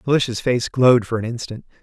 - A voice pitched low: Yes, low, 120 Hz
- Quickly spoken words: No, average, 195 wpm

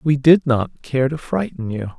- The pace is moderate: No, fast, 210 wpm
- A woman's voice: No, male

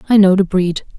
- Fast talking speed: Yes, fast, 245 wpm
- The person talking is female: Yes, female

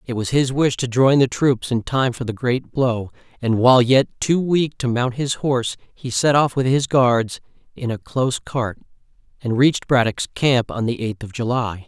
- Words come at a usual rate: No, fast, 220 wpm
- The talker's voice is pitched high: No, low, 125 Hz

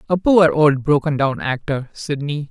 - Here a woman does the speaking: No, male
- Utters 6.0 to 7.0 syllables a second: No, 4.4 syllables/s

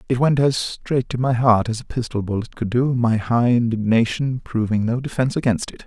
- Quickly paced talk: Yes, fast, 215 wpm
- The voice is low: Yes, low, 120 Hz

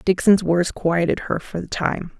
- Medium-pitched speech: Yes, medium, 180 Hz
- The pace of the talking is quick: No, average, 190 wpm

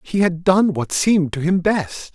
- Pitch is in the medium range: Yes, medium, 175 Hz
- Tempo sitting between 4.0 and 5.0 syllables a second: Yes, 4.4 syllables/s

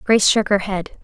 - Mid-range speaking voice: No, high, 200 Hz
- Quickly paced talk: Yes, fast, 230 wpm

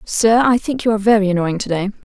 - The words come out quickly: Yes, fast, 255 wpm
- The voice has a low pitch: No, high, 210 Hz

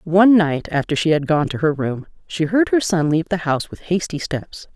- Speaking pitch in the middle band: Yes, medium, 165 Hz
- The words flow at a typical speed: No, fast, 240 wpm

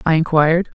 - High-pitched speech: No, medium, 160 Hz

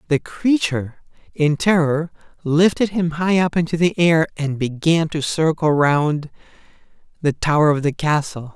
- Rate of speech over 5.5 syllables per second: No, 4.5 syllables/s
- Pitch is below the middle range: No, medium, 155 Hz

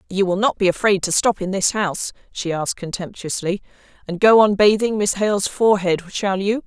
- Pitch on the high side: Yes, high, 195 Hz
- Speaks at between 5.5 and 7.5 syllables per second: Yes, 5.6 syllables/s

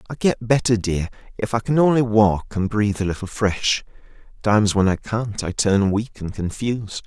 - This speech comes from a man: Yes, male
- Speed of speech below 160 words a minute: No, average, 195 wpm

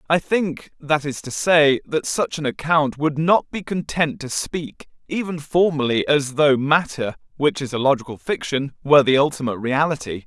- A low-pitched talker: No, medium, 145 Hz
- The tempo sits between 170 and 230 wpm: Yes, average, 175 wpm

